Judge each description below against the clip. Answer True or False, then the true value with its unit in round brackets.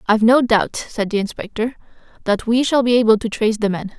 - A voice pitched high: True (225 Hz)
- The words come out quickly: True (225 wpm)